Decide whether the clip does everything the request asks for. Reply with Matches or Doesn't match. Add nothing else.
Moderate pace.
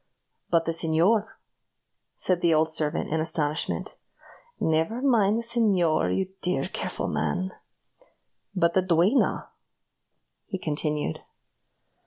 Doesn't match